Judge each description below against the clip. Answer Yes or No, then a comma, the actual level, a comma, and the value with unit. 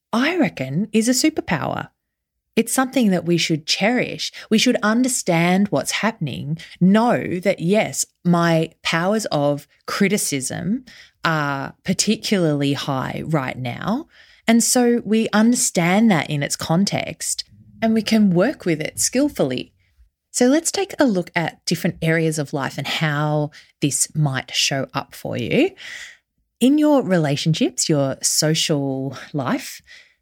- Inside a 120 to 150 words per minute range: Yes, slow, 135 wpm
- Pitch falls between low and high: Yes, medium, 180 Hz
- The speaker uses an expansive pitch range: Yes, wide, 7.2 semitones